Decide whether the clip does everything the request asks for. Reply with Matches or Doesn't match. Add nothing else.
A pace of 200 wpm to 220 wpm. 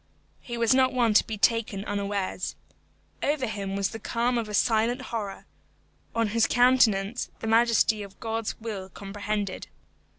Doesn't match